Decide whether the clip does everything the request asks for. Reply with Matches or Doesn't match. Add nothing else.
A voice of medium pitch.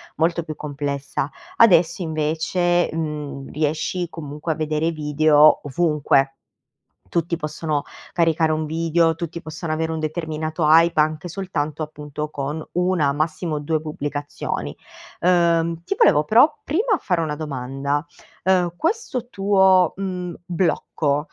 Matches